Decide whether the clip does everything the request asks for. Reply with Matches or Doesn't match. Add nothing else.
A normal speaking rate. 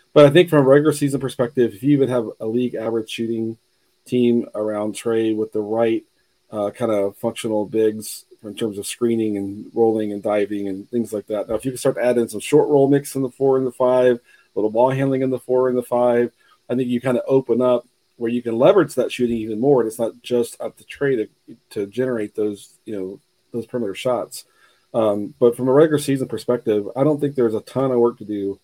Doesn't match